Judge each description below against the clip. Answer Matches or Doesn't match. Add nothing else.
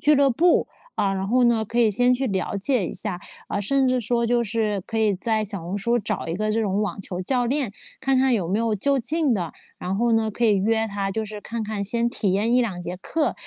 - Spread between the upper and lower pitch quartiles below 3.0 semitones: Doesn't match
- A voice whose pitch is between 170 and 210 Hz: Doesn't match